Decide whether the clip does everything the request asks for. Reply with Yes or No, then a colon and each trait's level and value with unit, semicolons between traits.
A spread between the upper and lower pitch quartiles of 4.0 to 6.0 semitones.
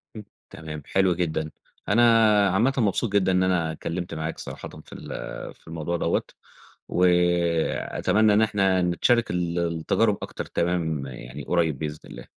No: average, 3.1 semitones